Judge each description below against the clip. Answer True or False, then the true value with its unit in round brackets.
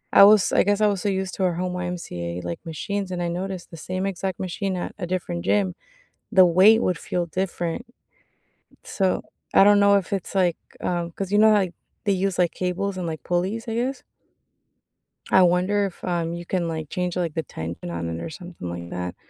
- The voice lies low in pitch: False (180 Hz)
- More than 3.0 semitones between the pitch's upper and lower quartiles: False (2.5 semitones)